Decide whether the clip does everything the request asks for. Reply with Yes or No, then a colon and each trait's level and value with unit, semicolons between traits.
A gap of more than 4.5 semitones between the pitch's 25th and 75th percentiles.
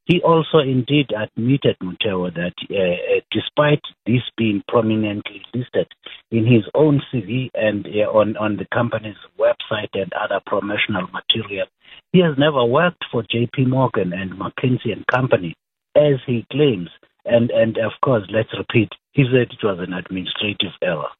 Yes: average, 4.9 semitones